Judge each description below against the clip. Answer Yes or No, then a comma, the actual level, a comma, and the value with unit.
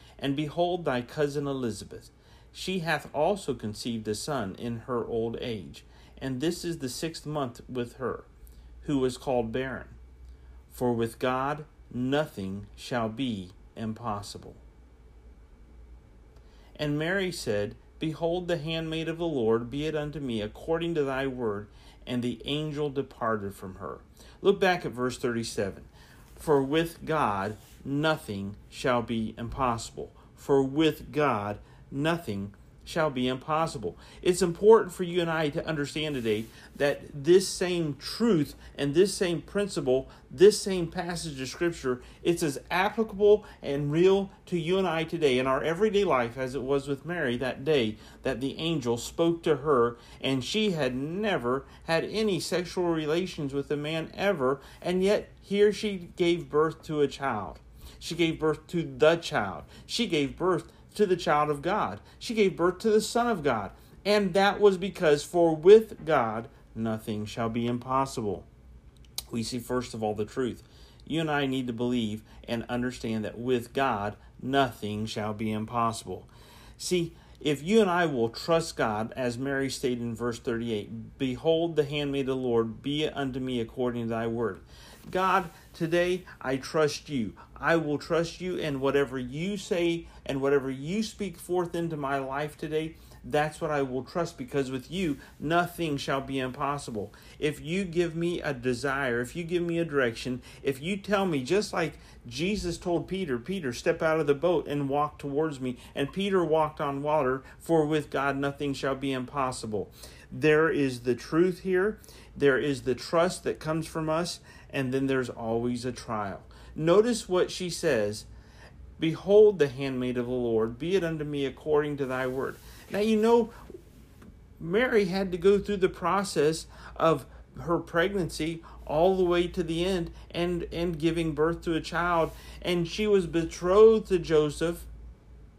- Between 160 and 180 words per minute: Yes, average, 165 wpm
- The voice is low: No, medium, 145 Hz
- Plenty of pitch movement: Yes, wide, 5.8 semitones